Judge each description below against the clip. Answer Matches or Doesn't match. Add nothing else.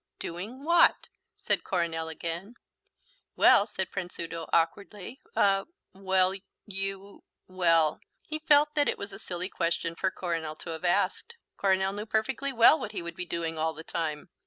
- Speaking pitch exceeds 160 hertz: Matches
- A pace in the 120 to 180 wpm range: Matches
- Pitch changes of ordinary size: Matches